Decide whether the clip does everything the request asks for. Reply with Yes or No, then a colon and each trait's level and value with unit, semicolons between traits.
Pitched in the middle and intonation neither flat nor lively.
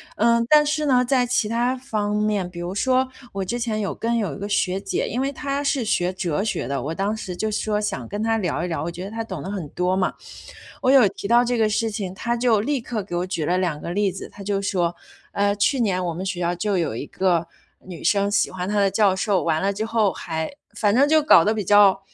No: high, 205 Hz; average, 3.9 semitones